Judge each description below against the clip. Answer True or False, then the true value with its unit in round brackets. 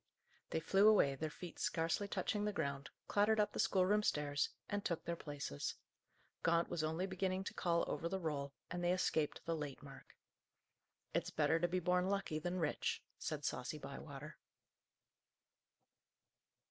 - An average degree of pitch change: True (4.0 semitones)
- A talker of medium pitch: True (170 Hz)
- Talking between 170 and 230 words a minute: False (160 wpm)